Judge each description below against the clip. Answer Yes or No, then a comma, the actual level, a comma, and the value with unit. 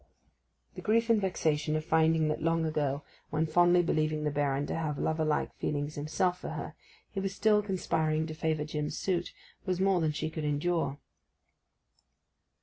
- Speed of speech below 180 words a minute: Yes, average, 170 wpm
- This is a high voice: No, medium, 160 Hz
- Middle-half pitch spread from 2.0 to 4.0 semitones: Yes, average, 2.7 semitones